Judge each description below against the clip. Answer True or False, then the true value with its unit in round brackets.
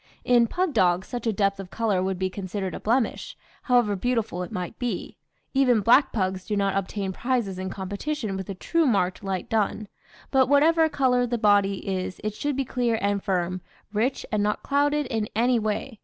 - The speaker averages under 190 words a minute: False (195 wpm)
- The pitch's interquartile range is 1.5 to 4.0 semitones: False (4.6 semitones)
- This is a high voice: True (215 Hz)